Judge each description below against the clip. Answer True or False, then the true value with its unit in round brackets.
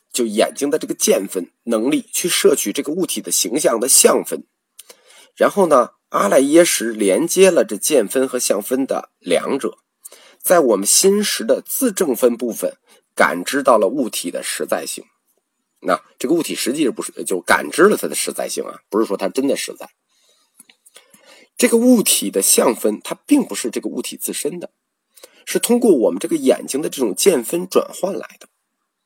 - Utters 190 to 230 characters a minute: False (260 characters per minute)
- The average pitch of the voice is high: True (230 Hz)